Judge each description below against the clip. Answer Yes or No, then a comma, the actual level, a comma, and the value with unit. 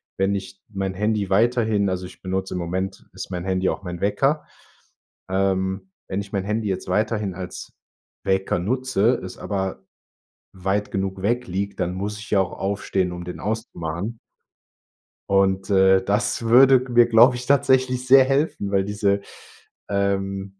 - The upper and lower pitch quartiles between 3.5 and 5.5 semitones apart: No, average, 2.8 semitones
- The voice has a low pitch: Yes, low, 100 Hz